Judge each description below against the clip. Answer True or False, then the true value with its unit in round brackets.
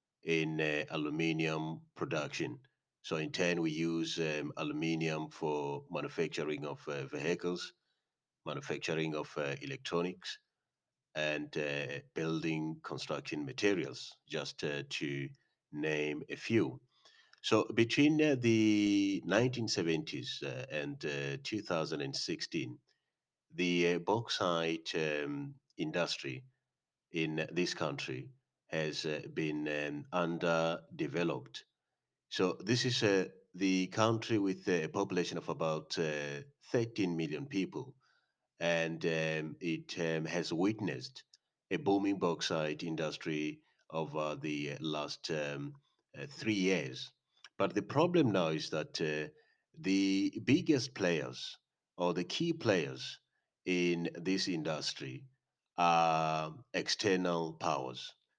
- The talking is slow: True (110 wpm)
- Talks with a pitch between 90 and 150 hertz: False (80 Hz)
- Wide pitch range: False (3.6 semitones)